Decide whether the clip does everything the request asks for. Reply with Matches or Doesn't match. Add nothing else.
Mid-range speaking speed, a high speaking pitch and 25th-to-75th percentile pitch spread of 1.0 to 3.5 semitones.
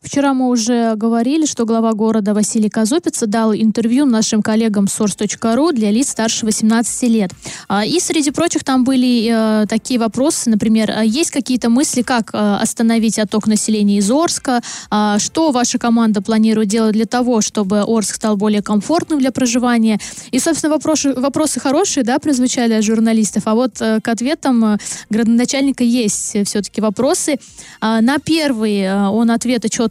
Matches